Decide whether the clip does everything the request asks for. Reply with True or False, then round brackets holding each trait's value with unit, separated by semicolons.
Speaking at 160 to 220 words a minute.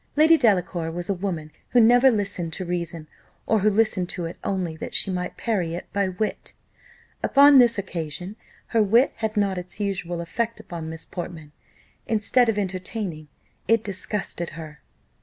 True (165 wpm)